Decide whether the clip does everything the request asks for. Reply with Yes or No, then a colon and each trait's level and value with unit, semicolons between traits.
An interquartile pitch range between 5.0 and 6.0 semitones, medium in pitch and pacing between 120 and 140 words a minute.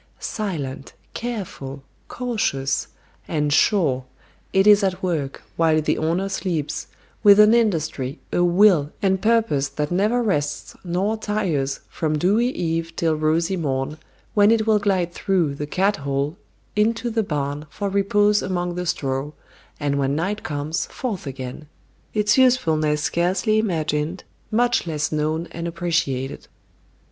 Yes: wide, 5.6 semitones; medium, 170 Hz; slow, 135 wpm